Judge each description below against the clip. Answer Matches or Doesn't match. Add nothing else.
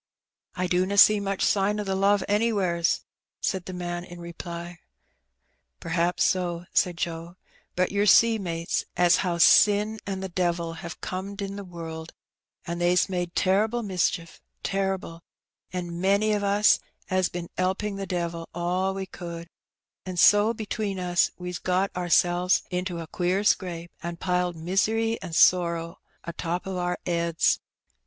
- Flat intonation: Matches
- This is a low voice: Doesn't match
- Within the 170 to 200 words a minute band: Doesn't match